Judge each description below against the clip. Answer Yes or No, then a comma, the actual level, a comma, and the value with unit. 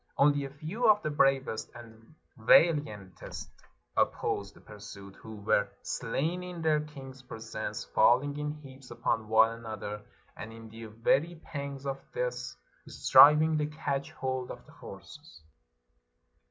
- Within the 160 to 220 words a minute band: No, average, 140 wpm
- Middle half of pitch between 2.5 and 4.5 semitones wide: No, average, 5.2 semitones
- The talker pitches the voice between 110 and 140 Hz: Yes, low, 135 Hz